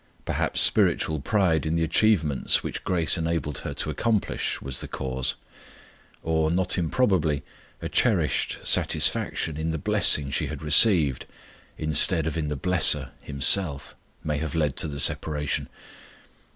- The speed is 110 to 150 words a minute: Yes, average, 140 wpm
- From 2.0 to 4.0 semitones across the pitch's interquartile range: Yes, narrow, 2.4 semitones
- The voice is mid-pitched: No, very low, 80 Hz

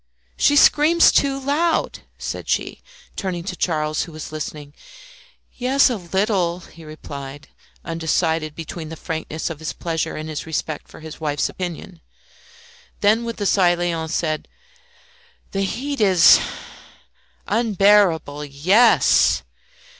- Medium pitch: Yes, medium, 170 Hz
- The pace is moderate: No, slow, 130 wpm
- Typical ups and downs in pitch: Yes, average, 4.8 semitones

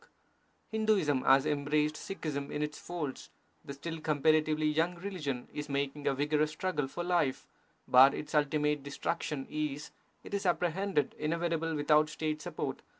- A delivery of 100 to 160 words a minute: Yes, average, 150 wpm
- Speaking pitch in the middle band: Yes, medium, 150 Hz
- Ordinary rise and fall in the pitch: No, narrow, 2.3 semitones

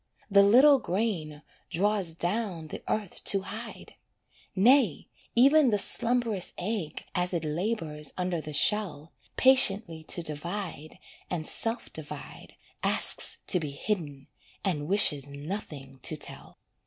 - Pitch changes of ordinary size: No, wide, 5.7 semitones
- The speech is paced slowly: Yes, slow, 125 wpm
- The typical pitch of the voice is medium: Yes, medium, 180 Hz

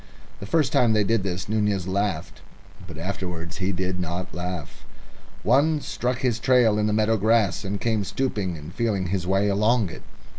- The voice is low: Yes, low, 100 Hz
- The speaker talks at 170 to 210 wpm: Yes, average, 180 wpm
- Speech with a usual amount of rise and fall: Yes, average, 3.6 semitones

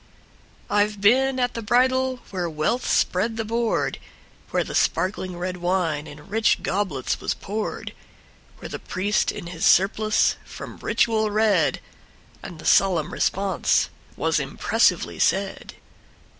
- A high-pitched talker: Yes, high, 205 Hz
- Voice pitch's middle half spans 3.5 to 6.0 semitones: Yes, average, 3.8 semitones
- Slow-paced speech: Yes, slow, 125 wpm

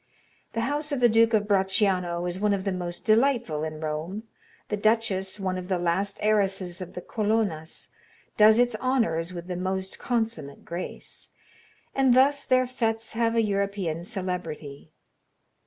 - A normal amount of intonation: Yes, average, 4.2 semitones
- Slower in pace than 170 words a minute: Yes, average, 155 wpm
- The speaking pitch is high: Yes, high, 200 Hz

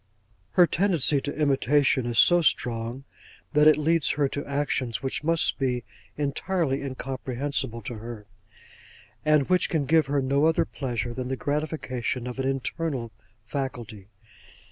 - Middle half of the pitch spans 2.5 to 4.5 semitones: Yes, average, 3.3 semitones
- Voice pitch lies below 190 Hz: Yes, low, 135 Hz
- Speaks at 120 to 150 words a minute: Yes, average, 145 wpm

